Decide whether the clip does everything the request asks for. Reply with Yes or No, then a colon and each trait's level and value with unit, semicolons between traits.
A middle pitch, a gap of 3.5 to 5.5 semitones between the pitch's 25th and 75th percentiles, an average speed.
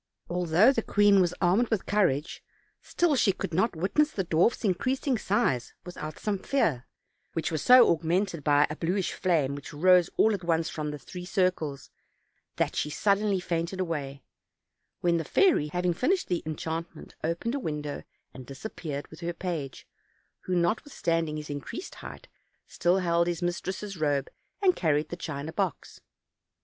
Yes: medium, 175 Hz; average, 4.1 semitones; average, 160 wpm